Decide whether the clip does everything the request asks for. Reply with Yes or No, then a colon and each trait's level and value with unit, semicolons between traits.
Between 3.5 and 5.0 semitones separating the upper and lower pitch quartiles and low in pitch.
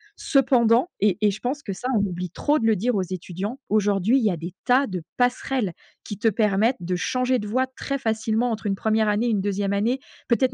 No: average, 3.9 semitones; high, 220 Hz